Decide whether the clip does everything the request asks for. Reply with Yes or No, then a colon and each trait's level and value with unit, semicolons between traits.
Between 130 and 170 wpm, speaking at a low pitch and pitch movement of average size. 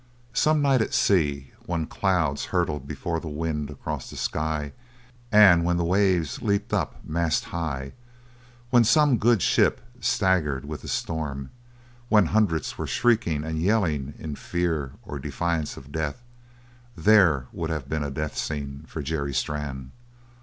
Yes: average, 150 wpm; very low, 80 Hz; average, 4.5 semitones